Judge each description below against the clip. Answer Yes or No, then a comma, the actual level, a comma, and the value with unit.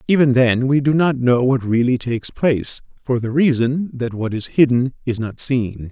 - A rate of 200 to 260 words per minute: Yes, fast, 205 wpm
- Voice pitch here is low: Yes, low, 125 Hz